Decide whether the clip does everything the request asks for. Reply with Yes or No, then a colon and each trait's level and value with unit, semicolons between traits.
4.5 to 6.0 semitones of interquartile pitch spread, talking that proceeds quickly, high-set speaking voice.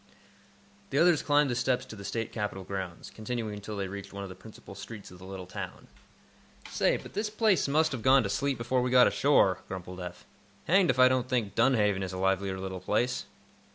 No: average, 5.2 semitones; fast, 215 wpm; low, 110 Hz